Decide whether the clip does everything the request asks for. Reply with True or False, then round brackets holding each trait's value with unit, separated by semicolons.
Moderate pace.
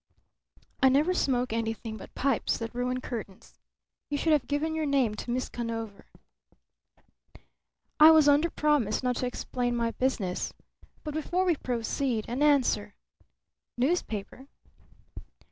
False (130 wpm)